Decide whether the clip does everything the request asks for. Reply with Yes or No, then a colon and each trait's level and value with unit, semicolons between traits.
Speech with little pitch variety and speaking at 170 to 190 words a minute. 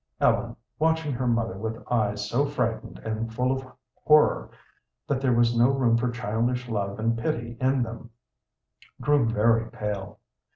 No: narrow, 2.3 semitones; average, 155 wpm